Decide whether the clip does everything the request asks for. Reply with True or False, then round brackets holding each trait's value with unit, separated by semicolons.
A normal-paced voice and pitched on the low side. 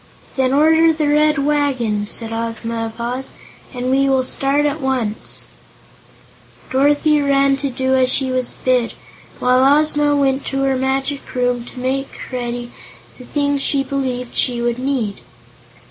False (150 wpm; 265 Hz)